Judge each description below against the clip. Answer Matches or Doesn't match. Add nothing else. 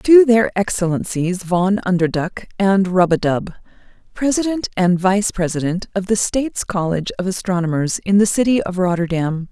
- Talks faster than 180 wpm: Doesn't match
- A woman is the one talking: Matches